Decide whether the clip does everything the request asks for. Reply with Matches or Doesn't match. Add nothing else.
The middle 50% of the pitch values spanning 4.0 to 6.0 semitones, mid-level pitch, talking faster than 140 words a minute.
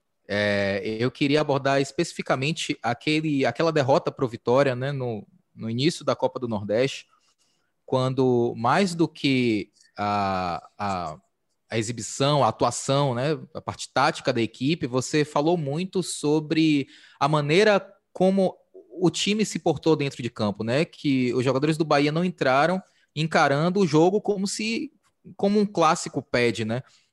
Matches